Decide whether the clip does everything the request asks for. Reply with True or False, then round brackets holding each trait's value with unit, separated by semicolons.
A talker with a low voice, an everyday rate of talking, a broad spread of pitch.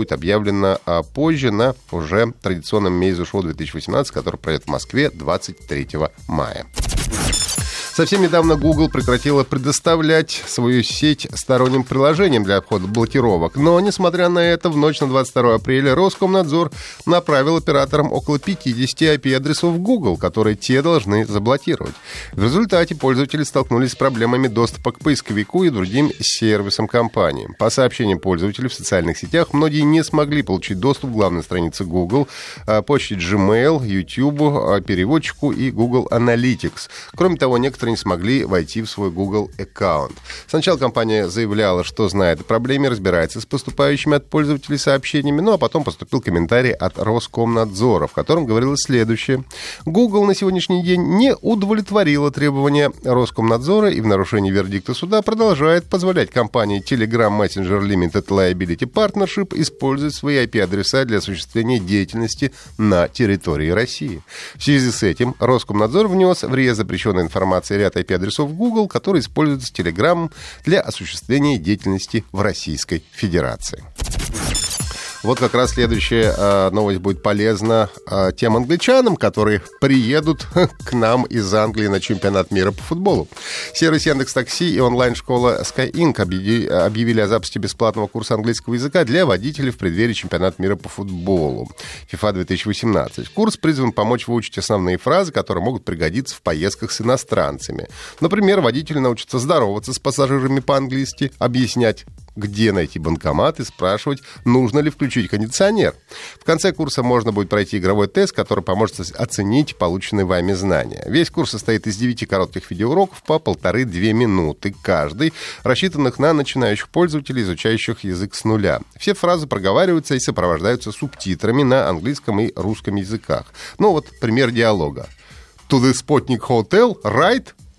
True (120 Hz; 140 wpm; 6.2 semitones)